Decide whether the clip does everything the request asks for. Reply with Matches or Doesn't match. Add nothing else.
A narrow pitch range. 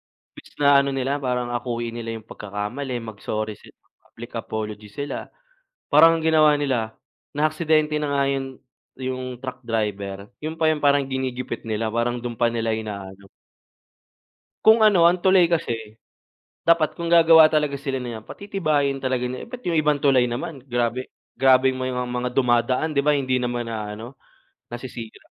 Doesn't match